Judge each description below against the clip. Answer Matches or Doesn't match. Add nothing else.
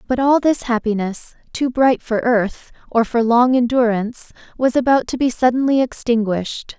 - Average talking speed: Matches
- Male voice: Doesn't match